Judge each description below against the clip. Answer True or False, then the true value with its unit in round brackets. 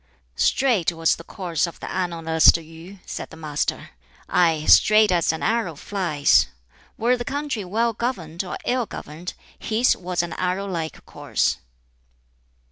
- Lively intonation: False (4.9 semitones)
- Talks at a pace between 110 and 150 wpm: True (145 wpm)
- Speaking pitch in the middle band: True (180 Hz)